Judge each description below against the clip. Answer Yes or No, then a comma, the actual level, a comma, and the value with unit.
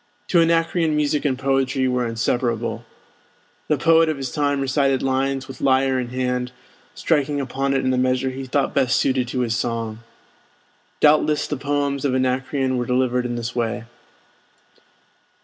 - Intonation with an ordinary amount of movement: No, narrow, 2.1 semitones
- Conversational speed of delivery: Yes, average, 165 wpm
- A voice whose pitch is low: Yes, low, 130 Hz